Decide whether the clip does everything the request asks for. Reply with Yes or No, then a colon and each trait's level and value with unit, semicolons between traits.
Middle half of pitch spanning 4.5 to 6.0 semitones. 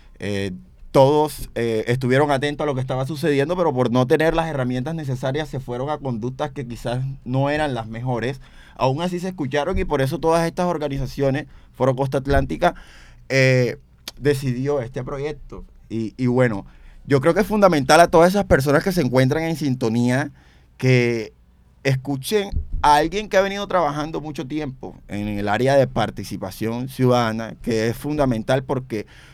No: average, 4.1 semitones